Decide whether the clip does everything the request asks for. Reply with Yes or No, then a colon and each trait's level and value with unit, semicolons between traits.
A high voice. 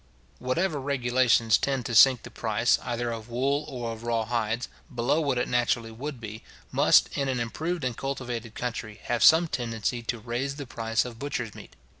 No: low, 120 Hz